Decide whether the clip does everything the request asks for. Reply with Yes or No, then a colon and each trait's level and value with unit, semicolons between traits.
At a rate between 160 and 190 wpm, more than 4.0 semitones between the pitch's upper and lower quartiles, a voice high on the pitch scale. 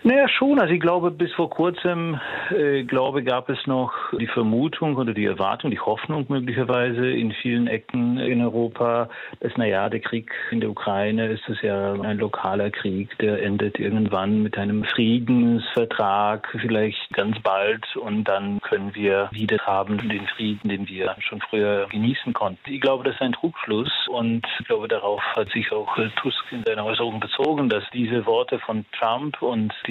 No: average, 175 wpm; average, 4.4 semitones; low, 115 Hz